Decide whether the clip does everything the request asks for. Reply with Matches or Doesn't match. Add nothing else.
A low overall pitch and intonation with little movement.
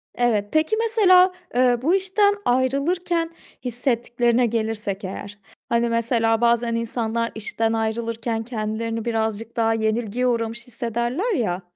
Doesn't match